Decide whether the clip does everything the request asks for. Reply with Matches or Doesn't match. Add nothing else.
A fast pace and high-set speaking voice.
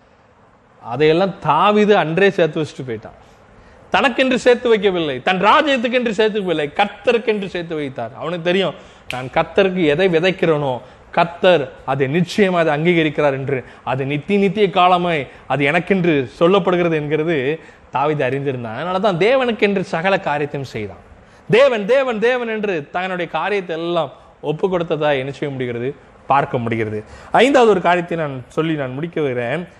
Doesn't match